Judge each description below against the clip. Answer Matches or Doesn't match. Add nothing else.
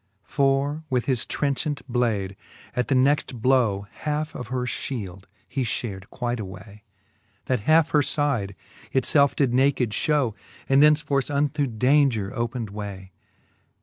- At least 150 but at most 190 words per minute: Doesn't match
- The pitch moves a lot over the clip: Doesn't match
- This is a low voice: Matches